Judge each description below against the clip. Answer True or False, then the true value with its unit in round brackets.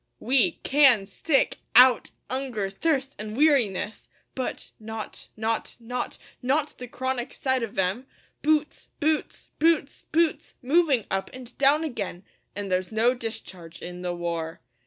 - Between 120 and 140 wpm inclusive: True (135 wpm)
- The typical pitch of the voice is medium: False (245 Hz)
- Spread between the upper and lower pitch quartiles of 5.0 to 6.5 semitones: True (5.3 semitones)